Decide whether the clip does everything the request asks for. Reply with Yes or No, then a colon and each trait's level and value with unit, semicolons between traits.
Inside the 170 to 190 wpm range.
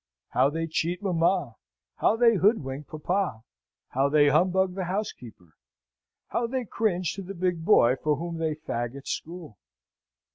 No: average, 150 wpm